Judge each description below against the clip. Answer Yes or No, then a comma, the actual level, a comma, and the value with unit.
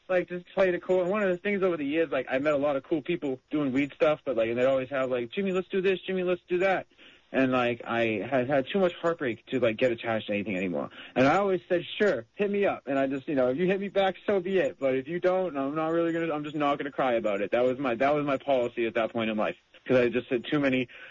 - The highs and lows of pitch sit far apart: Yes, wide, 6.1 semitones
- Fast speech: Yes, fast, 305 wpm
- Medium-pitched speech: Yes, medium, 150 Hz